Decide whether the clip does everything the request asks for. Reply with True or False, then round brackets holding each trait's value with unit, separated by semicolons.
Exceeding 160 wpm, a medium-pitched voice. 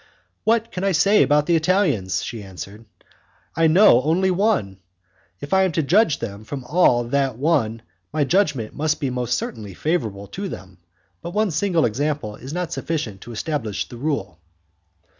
True (170 wpm; 145 Hz)